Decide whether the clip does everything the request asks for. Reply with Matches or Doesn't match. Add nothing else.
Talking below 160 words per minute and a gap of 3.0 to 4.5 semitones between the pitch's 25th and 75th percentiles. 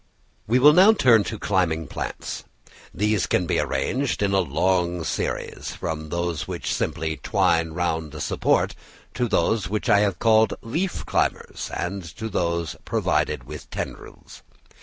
Doesn't match